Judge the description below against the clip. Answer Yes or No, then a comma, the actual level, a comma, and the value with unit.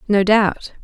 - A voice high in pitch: Yes, high, 205 Hz